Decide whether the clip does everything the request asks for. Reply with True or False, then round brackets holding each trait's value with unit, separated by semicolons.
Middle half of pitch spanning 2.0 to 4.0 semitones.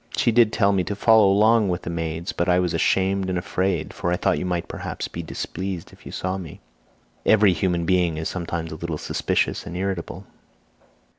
True (2.5 semitones)